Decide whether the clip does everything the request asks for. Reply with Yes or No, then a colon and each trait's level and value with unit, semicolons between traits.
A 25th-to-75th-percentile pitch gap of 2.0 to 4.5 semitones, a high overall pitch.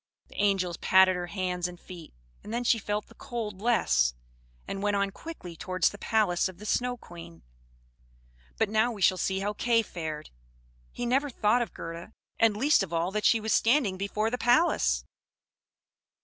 Yes: average, 4.2 semitones; high, 205 Hz